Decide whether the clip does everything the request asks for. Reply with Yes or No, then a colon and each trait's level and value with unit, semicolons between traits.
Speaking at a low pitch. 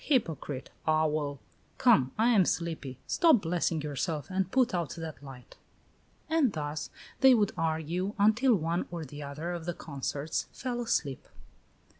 No: medium, 165 Hz